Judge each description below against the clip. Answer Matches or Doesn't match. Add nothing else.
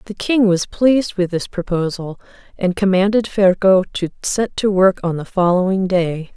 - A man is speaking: Doesn't match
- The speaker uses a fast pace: Doesn't match